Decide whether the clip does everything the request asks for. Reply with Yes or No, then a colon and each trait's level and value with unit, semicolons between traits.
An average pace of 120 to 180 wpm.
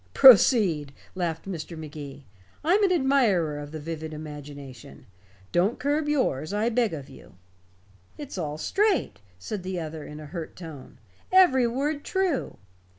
Yes: average, 145 wpm